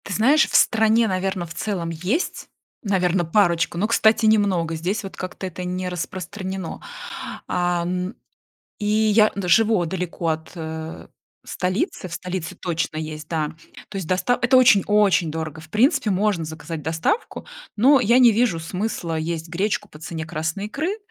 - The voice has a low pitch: No, medium, 185 Hz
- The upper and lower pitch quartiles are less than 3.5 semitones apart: No, average, 4.3 semitones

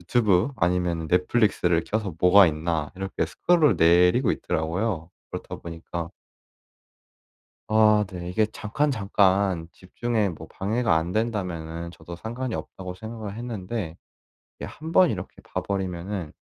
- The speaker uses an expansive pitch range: No, average, 4.3 semitones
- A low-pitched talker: Yes, very low, 95 Hz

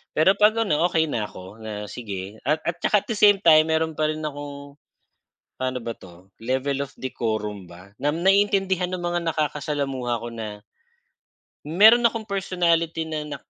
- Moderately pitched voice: Yes, medium, 150 Hz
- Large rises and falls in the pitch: Yes, wide, 6.9 semitones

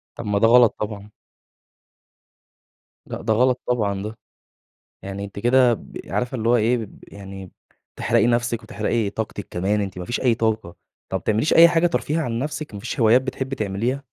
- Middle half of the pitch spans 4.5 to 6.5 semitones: No, average, 3.5 semitones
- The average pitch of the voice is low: Yes, low, 115 Hz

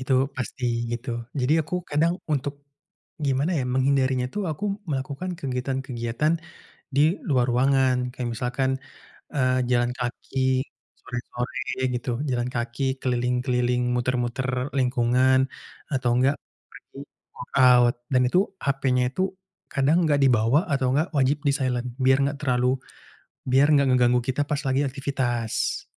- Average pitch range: No, narrow, 1.9 semitones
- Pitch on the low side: Yes, low, 130 Hz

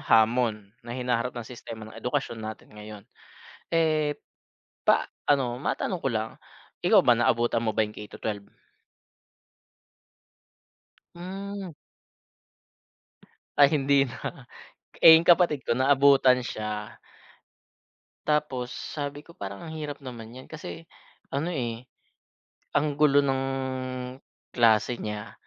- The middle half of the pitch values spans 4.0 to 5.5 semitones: Yes, average, 4.6 semitones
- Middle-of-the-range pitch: No, low, 130 Hz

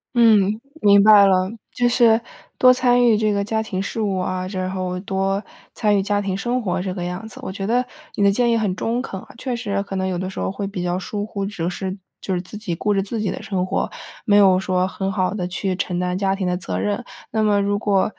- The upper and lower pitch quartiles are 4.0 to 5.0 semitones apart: No, narrow, 2.4 semitones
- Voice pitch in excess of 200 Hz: No, high, 195 Hz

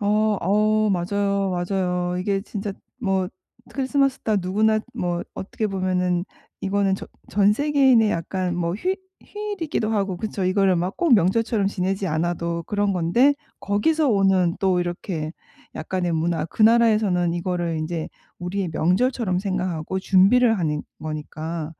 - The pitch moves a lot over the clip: No, average, 3.4 semitones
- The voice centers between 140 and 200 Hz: Yes, high, 190 Hz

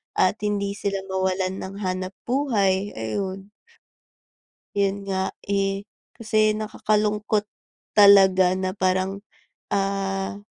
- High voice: Yes, high, 195 Hz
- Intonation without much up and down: Yes, narrow, 1.4 semitones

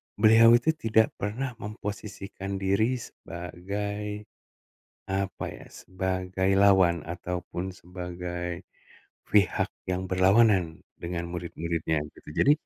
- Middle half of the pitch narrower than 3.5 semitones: Yes, average, 2.8 semitones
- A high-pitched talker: No, very low, 95 Hz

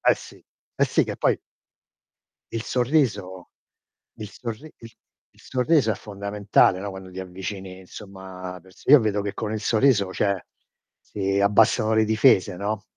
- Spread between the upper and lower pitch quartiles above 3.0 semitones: No, narrow, 2.5 semitones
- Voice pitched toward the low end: Yes, low, 100 Hz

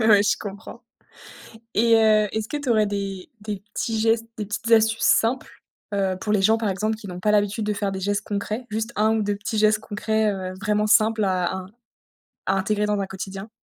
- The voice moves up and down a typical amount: No, narrow, 1.7 semitones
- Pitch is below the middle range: No, high, 210 Hz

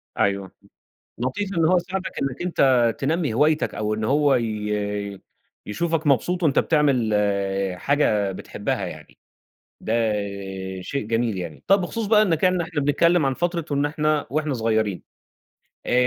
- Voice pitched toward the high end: No, medium, 140 Hz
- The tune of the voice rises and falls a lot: Yes, wide, 7.2 semitones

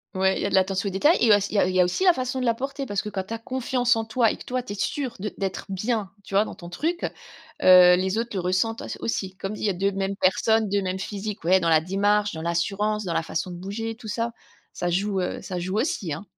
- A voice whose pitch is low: No, high, 200 Hz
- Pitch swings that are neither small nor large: Yes, average, 3.3 semitones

